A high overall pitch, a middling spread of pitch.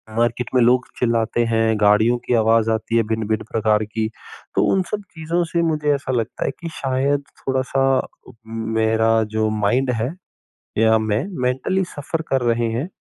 No: low, 115 Hz; average, 3.2 semitones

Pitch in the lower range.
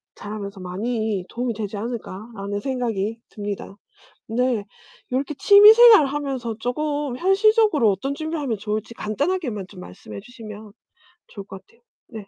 No: high, 230 Hz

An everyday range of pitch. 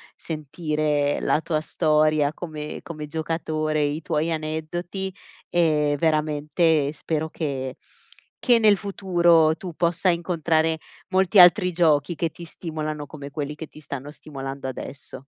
No: narrow, 2.2 semitones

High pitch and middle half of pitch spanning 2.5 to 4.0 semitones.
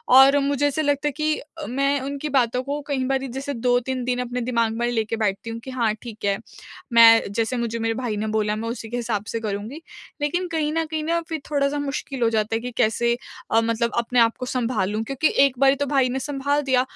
Yes: very high, 250 Hz; average, 3.7 semitones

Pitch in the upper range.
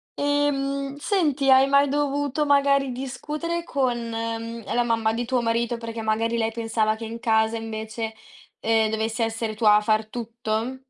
Yes: high, 235 Hz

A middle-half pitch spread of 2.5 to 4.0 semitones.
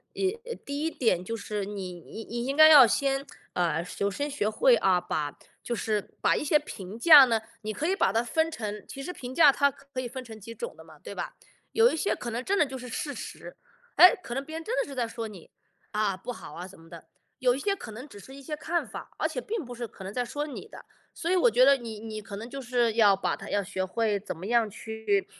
No: average, 5.3 semitones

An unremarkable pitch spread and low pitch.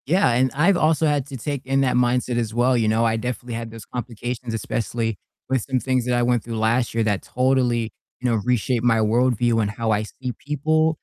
No: narrow, 2.3 semitones; low, 120 Hz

